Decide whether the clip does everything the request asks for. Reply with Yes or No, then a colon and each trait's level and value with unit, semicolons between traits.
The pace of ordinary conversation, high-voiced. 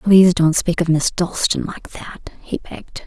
No: average, 195 wpm; medium, 170 Hz